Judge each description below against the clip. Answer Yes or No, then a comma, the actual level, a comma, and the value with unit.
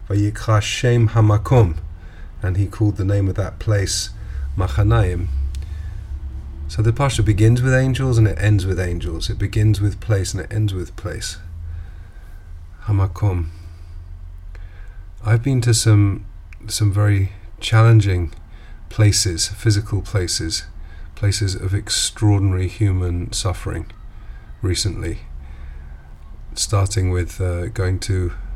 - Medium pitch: No, very low, 95 Hz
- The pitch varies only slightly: No, average, 3.8 semitones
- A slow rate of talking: Yes, slow, 110 wpm